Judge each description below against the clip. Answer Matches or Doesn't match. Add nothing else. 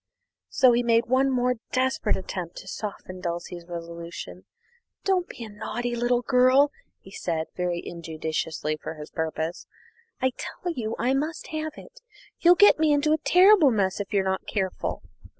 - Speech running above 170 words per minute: Doesn't match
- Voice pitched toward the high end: Matches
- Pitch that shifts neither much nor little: Doesn't match